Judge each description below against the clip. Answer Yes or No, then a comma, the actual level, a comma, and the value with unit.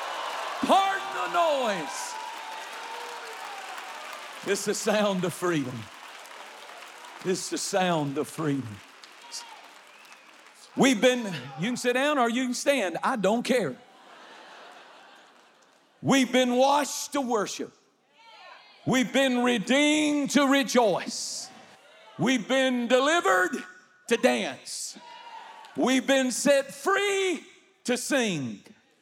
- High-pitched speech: Yes, very high, 255 Hz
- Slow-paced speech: Yes, slow, 95 wpm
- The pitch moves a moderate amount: No, wide, 6.4 semitones